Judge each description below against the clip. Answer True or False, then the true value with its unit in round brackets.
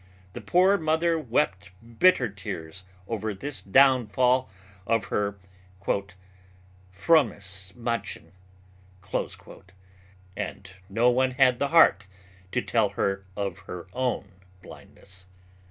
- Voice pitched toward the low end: True (105 Hz)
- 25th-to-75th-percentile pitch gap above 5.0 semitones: True (5.5 semitones)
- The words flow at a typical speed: False (100 wpm)